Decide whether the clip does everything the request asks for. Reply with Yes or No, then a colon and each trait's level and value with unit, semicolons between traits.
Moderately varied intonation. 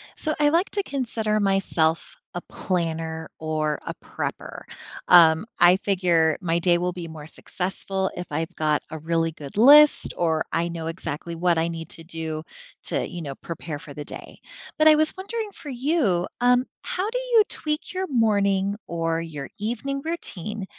No: wide, 7.2 semitones